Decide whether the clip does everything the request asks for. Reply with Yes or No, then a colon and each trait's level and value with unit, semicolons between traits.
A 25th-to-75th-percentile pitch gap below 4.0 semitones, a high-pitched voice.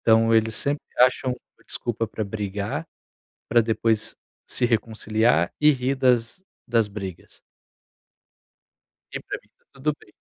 No: average, 2.7 semitones; low, 115 Hz